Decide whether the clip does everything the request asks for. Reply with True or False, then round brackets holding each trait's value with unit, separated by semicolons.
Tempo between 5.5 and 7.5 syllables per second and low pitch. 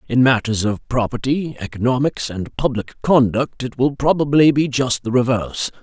False (5.0 syllables/s; 125 Hz)